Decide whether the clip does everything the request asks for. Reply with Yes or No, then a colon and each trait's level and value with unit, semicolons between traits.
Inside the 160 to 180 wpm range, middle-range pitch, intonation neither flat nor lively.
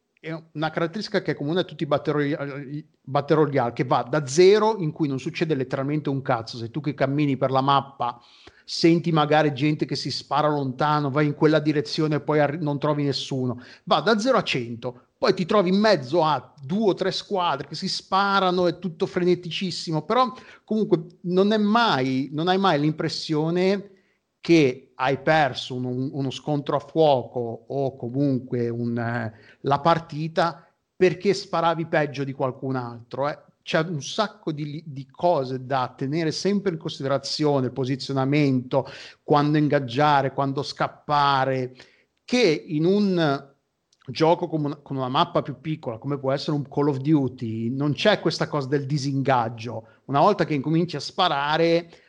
Yes: average, 165 wpm; medium, 150 Hz; average, 3.7 semitones